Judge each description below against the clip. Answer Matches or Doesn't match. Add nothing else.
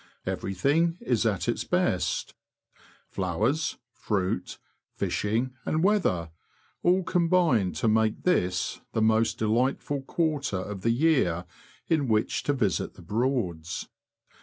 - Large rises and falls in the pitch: Matches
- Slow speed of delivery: Matches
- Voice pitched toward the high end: Doesn't match